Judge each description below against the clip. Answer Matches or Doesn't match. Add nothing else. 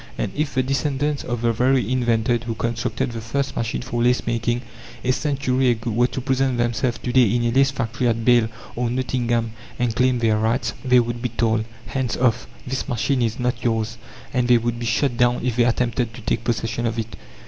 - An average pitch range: Doesn't match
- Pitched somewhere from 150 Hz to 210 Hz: Doesn't match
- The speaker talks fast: Matches